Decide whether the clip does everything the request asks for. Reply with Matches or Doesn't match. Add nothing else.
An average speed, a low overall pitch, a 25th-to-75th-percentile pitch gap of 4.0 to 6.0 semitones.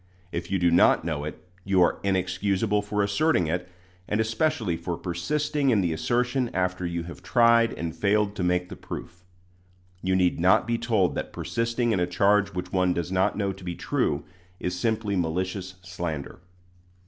Doesn't match